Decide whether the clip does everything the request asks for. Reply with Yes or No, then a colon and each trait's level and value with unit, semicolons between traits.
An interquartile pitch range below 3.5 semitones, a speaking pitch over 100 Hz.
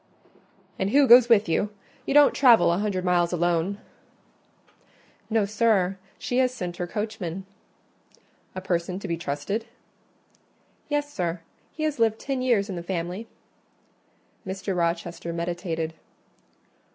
No: average, 4.7 semitones; high, 190 Hz